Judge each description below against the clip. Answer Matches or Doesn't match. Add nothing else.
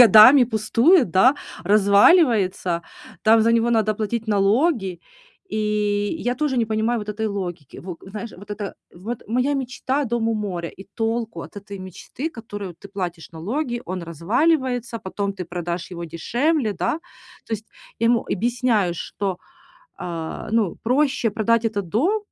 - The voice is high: Matches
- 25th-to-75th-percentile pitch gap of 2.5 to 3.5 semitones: Doesn't match